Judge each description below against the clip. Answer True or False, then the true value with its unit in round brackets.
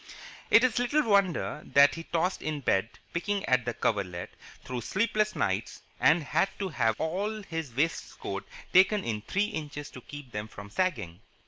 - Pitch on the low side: False (155 Hz)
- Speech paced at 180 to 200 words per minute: False (165 wpm)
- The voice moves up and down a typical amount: False (8.6 semitones)